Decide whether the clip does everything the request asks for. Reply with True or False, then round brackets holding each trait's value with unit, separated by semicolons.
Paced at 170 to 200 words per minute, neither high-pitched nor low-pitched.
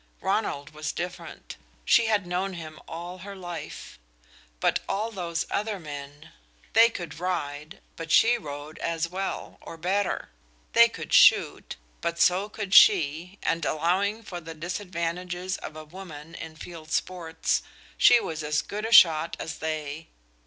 False (150 wpm; 170 Hz)